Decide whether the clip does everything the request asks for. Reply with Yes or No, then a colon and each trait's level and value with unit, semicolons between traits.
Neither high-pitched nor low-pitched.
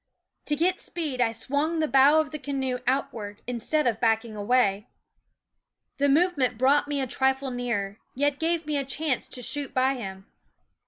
No: very high, 265 Hz